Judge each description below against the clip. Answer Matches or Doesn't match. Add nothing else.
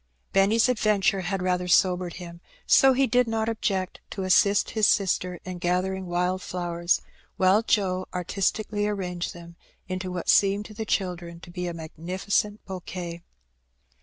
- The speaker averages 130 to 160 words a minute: Matches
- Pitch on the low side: Doesn't match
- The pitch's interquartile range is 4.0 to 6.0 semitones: Doesn't match